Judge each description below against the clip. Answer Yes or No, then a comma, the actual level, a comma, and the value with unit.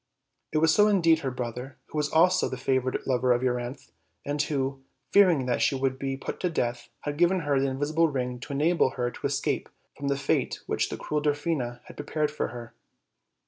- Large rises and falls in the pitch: No, average, 3.4 semitones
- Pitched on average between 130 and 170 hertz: Yes, medium, 140 Hz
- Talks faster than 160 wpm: Yes, average, 200 wpm